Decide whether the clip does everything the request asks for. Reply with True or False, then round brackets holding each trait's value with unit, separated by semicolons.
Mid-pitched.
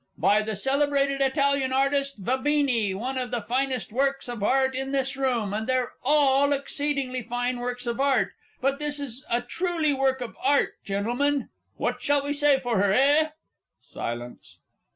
False (265 Hz)